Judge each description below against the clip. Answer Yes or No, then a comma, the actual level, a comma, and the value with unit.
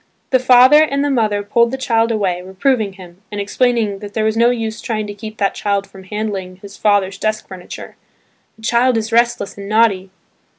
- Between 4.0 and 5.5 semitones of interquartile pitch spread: No, average, 2.9 semitones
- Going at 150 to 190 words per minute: No, average, 200 wpm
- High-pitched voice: Yes, high, 215 Hz